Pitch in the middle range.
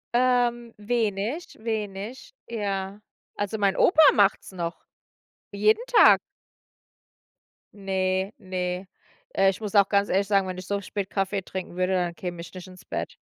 No: high, 195 Hz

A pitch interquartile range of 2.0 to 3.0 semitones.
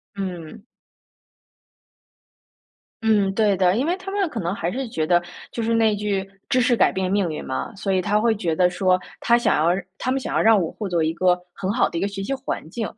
No: average, 4.1 semitones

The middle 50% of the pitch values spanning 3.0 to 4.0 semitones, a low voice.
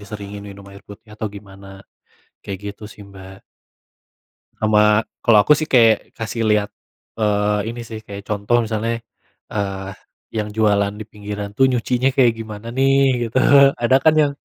No: narrow, 2.4 semitones; low, 105 Hz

